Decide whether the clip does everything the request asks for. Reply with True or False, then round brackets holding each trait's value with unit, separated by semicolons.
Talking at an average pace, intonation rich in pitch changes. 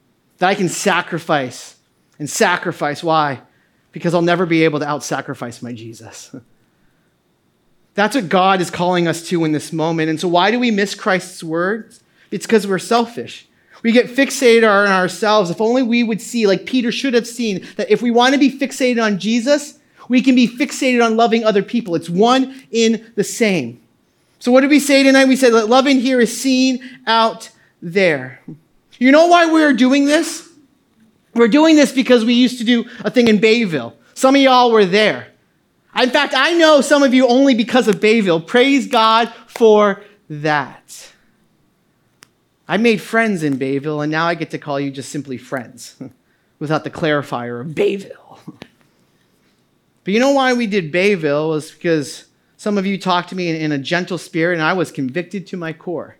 True (185 wpm; 6.9 semitones)